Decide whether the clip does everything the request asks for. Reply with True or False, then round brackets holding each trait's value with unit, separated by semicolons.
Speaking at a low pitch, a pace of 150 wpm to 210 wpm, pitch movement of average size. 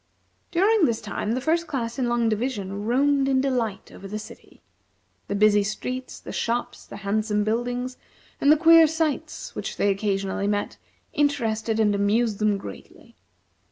False (230 Hz; 155 wpm; 4.4 semitones)